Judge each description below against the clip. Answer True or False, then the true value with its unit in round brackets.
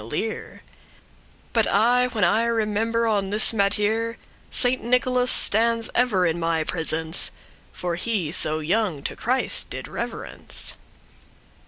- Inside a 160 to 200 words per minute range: False (135 wpm)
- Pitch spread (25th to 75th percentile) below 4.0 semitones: False (4.7 semitones)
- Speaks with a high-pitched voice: True (215 Hz)